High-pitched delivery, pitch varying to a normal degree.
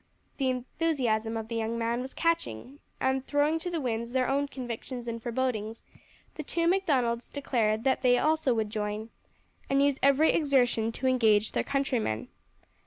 Yes: very high, 255 Hz; average, 3.7 semitones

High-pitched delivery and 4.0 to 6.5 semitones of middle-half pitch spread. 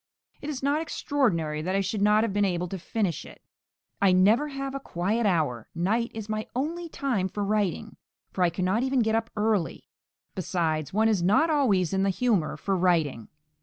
Yes: high, 205 Hz; average, 4.6 semitones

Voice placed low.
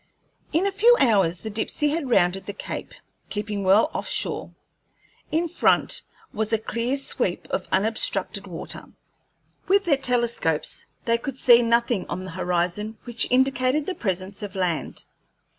No: high, 225 Hz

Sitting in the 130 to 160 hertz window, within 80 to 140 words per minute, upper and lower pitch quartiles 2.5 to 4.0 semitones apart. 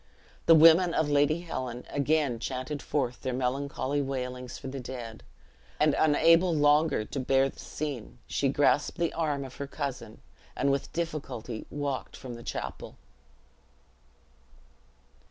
Yes: medium, 140 Hz; slow, 135 wpm; average, 2.9 semitones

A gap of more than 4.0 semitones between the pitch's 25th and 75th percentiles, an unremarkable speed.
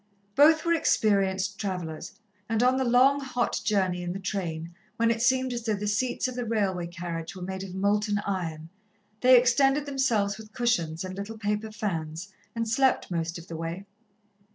Yes: average, 5.2 semitones; average, 180 wpm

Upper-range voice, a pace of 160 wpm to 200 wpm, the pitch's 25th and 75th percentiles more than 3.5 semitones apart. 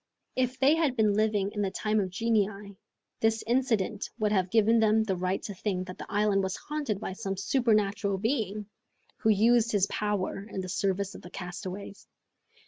No: high, 210 Hz; average, 185 wpm; narrow, 2.4 semitones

